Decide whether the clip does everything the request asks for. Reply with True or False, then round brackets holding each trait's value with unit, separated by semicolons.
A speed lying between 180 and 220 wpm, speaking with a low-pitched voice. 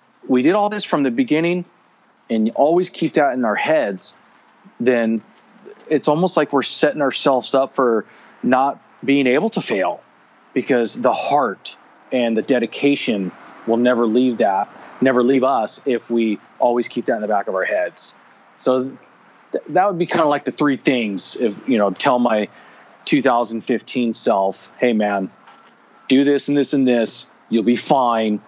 False (170 wpm; 130 Hz)